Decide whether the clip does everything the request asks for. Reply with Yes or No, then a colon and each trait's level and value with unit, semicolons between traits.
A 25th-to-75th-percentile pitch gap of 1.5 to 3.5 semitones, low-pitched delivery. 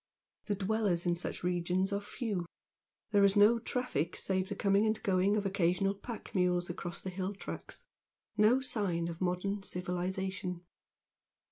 No: narrow, 2.4 semitones; high, 190 Hz